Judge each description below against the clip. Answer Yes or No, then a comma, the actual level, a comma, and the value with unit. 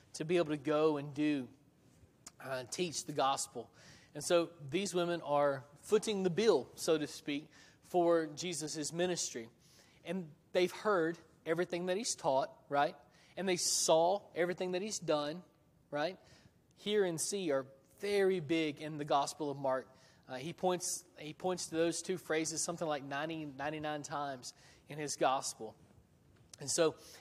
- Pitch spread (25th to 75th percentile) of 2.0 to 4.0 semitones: Yes, average, 3.5 semitones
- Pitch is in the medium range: Yes, medium, 155 Hz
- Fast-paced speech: No, average, 155 wpm